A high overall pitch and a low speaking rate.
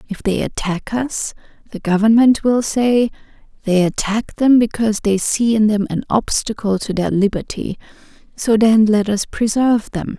No: high, 215 Hz; average, 160 wpm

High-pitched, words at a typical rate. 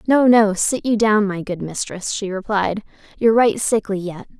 Yes: high, 205 Hz; average, 190 wpm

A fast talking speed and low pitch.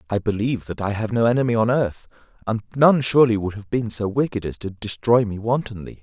Yes: fast, 220 wpm; low, 110 Hz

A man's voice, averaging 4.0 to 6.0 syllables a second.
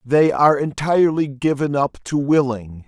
Yes: male; 4.8 syllables/s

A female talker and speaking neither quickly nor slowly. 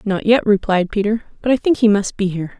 No: female; fast, 255 wpm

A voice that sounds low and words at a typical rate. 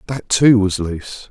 Yes: low, 105 Hz; average, 185 wpm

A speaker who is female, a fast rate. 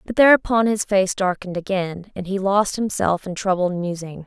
No: female; average, 185 wpm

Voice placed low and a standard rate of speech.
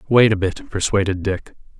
Yes: low, 105 Hz; average, 165 wpm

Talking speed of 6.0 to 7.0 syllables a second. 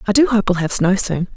Yes: 6.3 syllables/s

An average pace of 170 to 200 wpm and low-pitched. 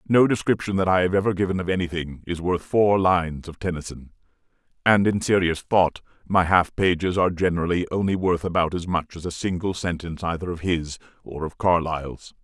Yes: average, 190 wpm; very low, 90 Hz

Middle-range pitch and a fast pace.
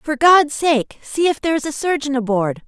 No: very high, 285 Hz; fast, 225 wpm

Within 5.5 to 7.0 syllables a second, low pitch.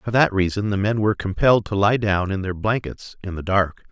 Yes: 5.7 syllables/s; low, 100 Hz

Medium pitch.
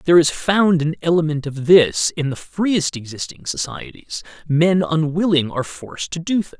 Yes: medium, 150 Hz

